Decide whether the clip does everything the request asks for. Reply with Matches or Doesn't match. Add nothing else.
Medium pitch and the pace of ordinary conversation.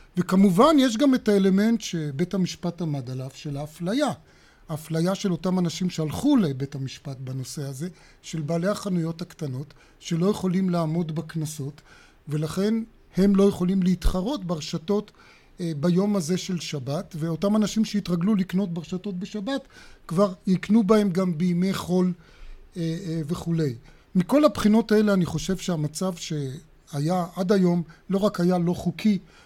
Matches